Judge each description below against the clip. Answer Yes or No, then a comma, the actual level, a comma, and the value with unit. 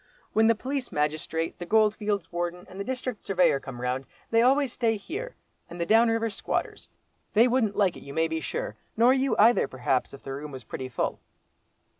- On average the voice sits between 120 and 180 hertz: No, high, 205 Hz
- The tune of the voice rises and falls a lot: Yes, wide, 7.1 semitones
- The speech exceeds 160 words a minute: Yes, average, 200 wpm